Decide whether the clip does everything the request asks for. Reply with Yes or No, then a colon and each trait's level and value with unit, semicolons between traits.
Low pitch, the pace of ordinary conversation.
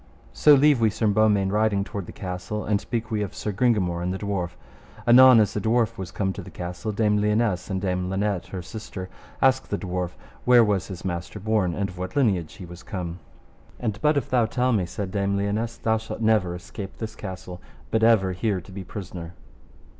No: low, 100 Hz; fast, 210 wpm